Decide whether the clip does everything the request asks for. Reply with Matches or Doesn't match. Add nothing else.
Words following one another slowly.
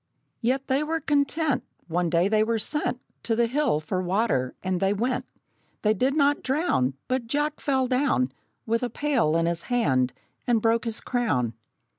Doesn't match